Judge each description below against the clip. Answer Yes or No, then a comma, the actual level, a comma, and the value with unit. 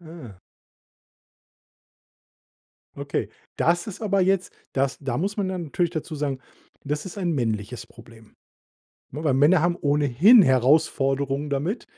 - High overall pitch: No, medium, 150 Hz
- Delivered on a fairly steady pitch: No, average, 4.7 semitones